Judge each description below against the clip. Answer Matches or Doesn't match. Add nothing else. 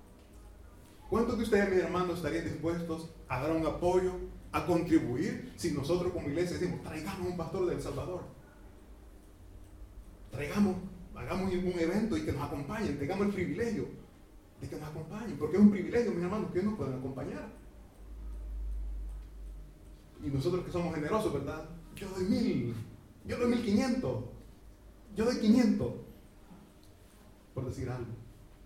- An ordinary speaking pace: Matches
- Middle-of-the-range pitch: Matches